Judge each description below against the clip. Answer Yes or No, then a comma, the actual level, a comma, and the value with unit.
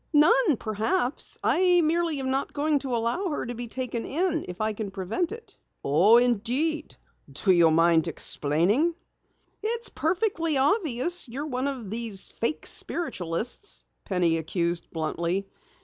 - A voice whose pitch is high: Yes, high, 245 Hz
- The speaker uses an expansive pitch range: Yes, wide, 8.7 semitones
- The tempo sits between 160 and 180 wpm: No, average, 145 wpm